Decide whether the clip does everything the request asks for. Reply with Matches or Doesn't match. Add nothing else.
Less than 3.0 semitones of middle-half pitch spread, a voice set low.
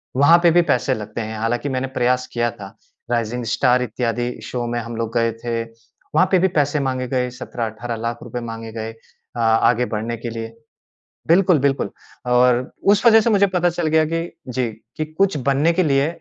Doesn't match